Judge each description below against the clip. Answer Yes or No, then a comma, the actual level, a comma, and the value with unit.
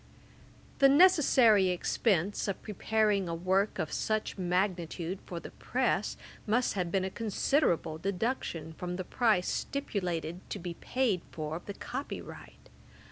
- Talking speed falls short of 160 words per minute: Yes, slow, 135 wpm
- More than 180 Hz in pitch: Yes, high, 190 Hz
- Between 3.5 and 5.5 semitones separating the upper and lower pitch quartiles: Yes, average, 4.0 semitones